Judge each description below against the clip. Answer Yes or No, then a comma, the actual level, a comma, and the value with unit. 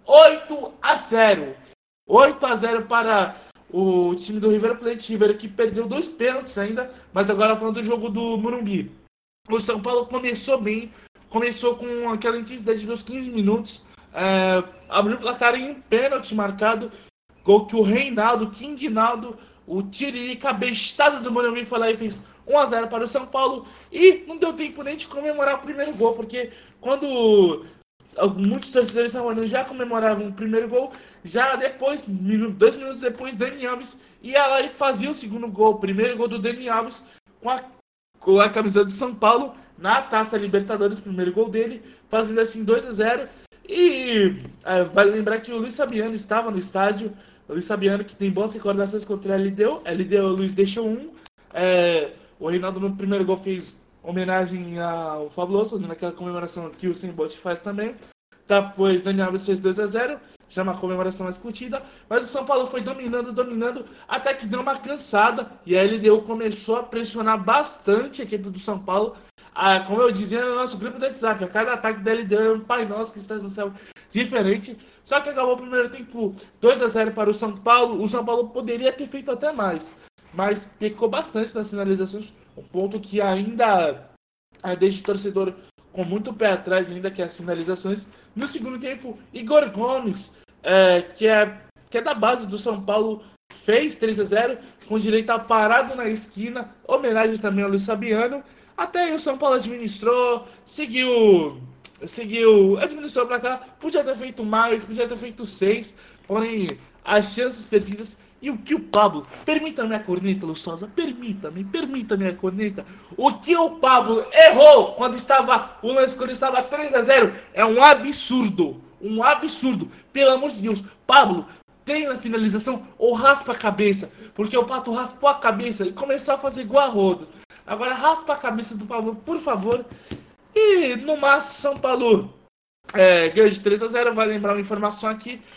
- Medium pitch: No, high, 225 Hz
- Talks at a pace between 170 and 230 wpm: Yes, average, 180 wpm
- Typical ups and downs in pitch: Yes, average, 3.6 semitones